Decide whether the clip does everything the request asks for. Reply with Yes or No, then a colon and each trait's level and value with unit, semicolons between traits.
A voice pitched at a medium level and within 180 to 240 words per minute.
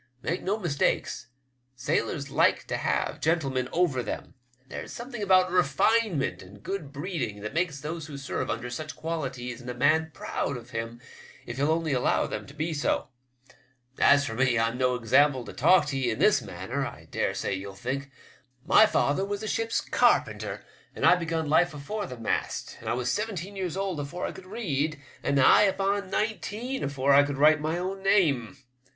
Yes: medium, 150 Hz; average, 195 wpm